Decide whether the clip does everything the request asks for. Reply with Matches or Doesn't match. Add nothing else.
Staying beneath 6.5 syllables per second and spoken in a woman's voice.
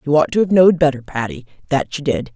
Doesn't match